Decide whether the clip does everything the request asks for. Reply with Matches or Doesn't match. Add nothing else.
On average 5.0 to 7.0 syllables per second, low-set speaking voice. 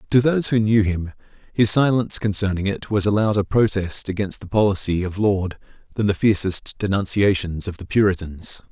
Matches